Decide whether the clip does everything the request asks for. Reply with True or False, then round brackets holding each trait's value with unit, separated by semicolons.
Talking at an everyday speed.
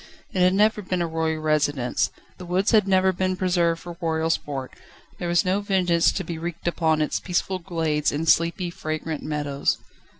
True (185 wpm)